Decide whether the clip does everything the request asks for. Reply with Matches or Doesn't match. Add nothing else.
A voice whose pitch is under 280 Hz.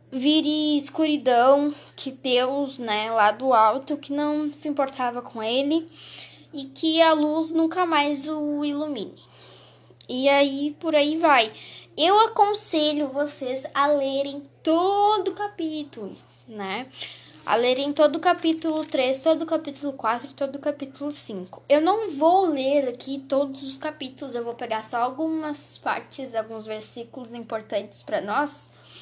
Doesn't match